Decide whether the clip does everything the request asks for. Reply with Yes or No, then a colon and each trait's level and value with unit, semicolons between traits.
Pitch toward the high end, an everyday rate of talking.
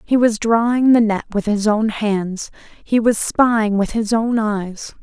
Yes: high, 220 Hz; average, 190 wpm